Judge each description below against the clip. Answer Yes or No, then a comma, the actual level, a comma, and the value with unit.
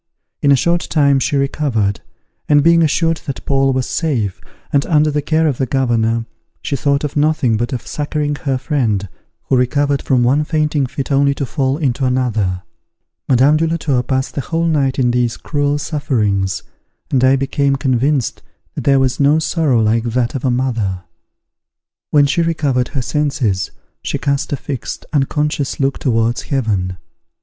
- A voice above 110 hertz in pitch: Yes, low, 135 Hz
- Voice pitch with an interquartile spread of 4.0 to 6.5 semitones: No, average, 3.1 semitones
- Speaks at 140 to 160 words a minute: No, average, 175 wpm